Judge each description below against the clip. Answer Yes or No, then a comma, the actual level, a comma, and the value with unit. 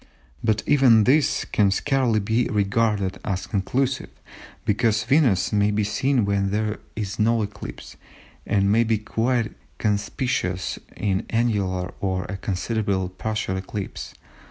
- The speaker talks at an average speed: No, slow, 130 wpm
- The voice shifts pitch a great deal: No, average, 2.8 semitones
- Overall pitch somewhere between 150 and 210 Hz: No, low, 105 Hz